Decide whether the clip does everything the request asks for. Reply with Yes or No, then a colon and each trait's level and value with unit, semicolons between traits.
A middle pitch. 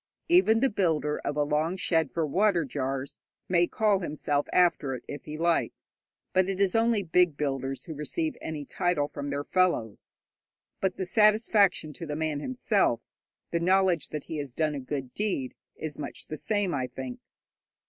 Yes: medium, 160 Hz